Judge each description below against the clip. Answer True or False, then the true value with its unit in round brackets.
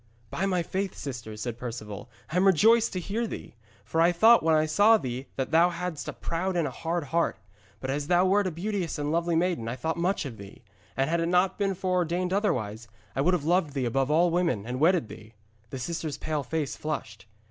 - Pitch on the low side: False (165 Hz)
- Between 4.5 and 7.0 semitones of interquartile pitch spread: True (5.3 semitones)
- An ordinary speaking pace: False (225 wpm)